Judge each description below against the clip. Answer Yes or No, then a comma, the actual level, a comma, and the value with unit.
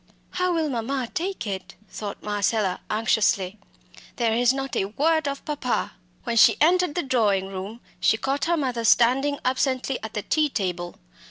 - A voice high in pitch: Yes, high, 245 Hz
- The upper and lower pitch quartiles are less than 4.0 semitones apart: No, average, 5.2 semitones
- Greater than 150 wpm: Yes, average, 165 wpm